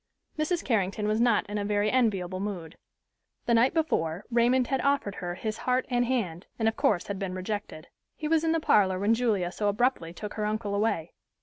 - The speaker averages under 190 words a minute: No, fast, 205 wpm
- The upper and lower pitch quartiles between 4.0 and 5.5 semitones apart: Yes, average, 4.4 semitones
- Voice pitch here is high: Yes, high, 210 Hz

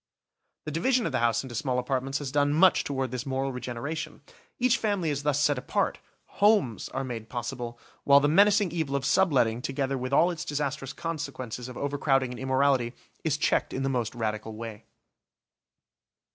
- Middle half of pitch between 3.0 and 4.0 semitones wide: Yes, average, 3.3 semitones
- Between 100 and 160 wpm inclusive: No, average, 175 wpm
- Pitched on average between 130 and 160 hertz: Yes, low, 135 Hz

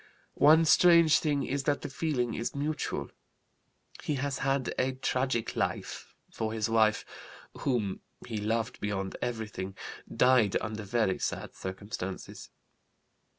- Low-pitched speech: Yes, low, 120 Hz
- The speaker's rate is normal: No, slow, 125 wpm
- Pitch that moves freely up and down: No, average, 4.5 semitones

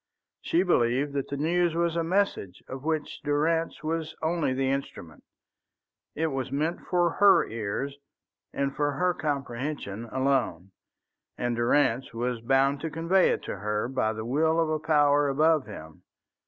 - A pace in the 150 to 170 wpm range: Yes, average, 155 wpm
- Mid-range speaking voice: Yes, medium, 145 Hz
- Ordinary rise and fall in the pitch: Yes, average, 4.6 semitones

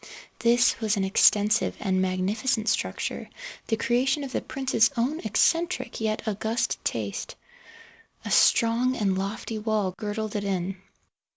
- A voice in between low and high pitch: No, high, 220 Hz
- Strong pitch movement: No, average, 3.1 semitones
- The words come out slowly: Yes, slow, 130 wpm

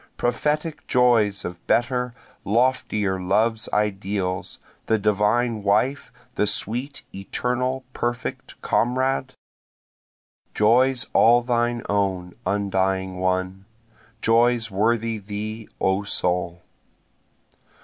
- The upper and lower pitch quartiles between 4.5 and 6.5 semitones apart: No, average, 3.9 semitones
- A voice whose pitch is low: Yes, low, 110 Hz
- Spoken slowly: Yes, slow, 85 wpm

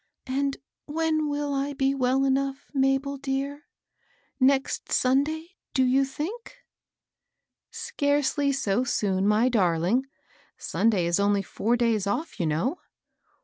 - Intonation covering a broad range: No, average, 3.9 semitones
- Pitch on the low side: No, very high, 270 Hz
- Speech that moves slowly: Yes, slow, 130 wpm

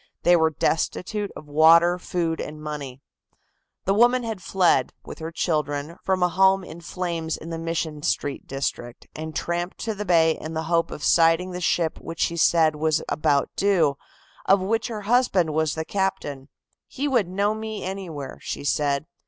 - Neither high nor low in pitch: Yes, medium, 165 Hz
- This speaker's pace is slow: No, average, 175 wpm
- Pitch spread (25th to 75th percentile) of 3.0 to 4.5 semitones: Yes, average, 3.7 semitones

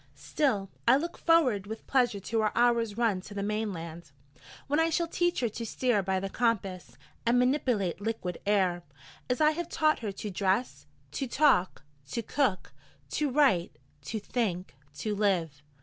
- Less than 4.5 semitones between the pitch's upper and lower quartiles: No, average, 5.1 semitones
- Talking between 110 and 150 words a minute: No, average, 165 wpm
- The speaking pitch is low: No, high, 220 Hz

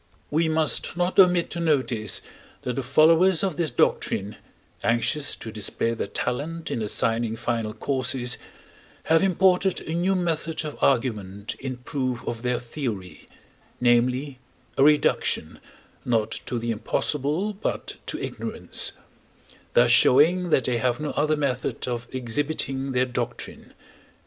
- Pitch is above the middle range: No, low, 130 Hz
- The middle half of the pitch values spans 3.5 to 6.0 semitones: Yes, average, 5.0 semitones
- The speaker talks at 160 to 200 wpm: No, slow, 135 wpm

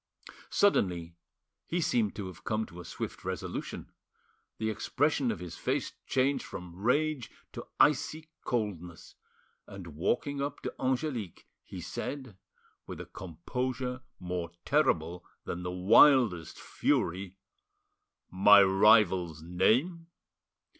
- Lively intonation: Yes, wide, 6.7 semitones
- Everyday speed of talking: No, slow, 115 wpm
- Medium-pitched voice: No, low, 105 Hz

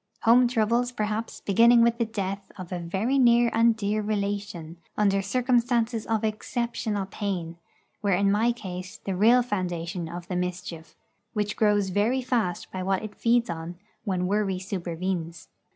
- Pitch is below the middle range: No, high, 205 Hz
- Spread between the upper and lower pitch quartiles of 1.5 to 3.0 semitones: No, average, 4.0 semitones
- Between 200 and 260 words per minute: No, average, 155 wpm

